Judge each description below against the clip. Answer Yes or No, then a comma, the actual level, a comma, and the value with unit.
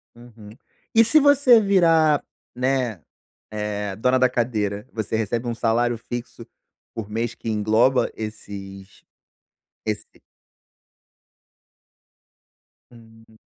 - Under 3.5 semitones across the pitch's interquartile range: Yes, average, 3.1 semitones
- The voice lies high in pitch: No, low, 115 Hz